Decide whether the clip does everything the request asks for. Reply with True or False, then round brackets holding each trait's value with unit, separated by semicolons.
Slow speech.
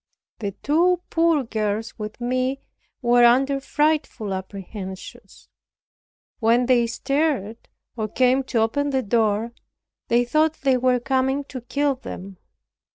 True (125 wpm)